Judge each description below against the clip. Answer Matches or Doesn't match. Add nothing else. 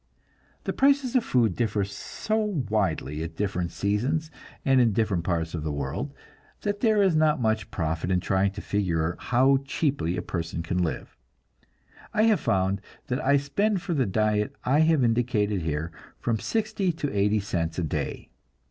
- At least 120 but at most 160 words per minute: Doesn't match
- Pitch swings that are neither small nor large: Doesn't match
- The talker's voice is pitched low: Matches